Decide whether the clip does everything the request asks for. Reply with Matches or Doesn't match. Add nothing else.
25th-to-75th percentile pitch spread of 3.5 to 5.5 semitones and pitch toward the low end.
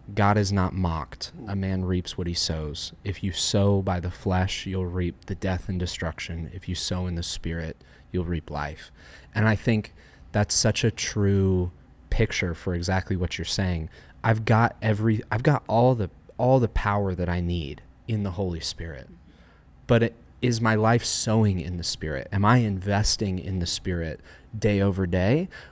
Matches